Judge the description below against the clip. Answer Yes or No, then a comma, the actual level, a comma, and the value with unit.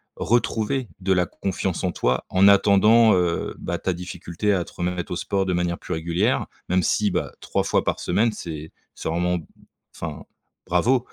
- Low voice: Yes, very low, 90 Hz